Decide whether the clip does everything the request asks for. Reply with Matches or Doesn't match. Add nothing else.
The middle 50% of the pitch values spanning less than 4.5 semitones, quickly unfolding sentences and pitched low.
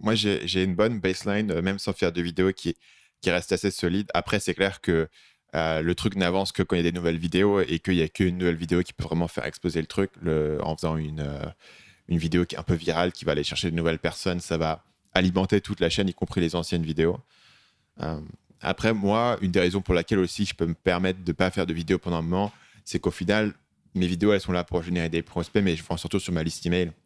Matches